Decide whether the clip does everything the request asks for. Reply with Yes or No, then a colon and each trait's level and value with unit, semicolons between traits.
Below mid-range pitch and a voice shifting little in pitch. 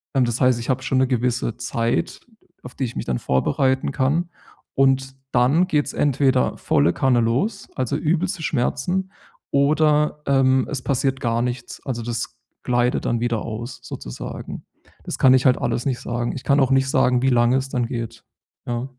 Yes: low, 130 Hz; narrow, 2.3 semitones